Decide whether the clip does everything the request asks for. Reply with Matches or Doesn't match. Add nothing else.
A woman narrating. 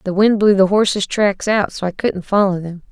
Matches